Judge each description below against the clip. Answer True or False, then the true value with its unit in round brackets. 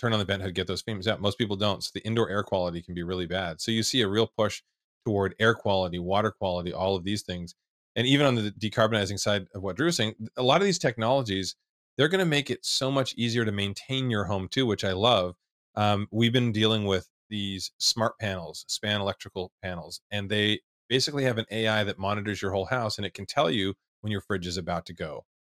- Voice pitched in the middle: False (105 Hz)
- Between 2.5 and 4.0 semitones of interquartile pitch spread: True (2.9 semitones)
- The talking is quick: True (240 wpm)